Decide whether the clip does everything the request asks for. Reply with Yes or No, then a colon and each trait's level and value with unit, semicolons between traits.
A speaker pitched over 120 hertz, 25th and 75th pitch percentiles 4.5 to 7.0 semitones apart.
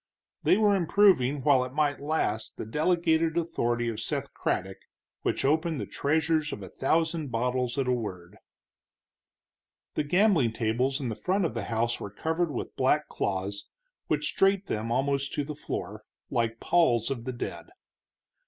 Yes: low, 135 Hz; wide, 5.6 semitones